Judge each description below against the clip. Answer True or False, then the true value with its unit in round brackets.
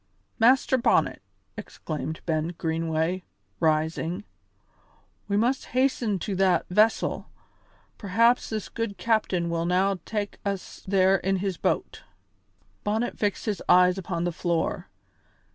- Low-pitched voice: False (190 Hz)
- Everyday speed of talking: False (120 wpm)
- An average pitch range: True (4.0 semitones)